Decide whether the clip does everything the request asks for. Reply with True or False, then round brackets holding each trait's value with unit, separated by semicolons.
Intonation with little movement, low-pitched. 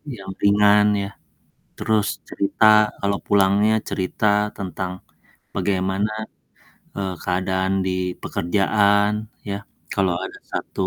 True (1.5 semitones; 100 Hz)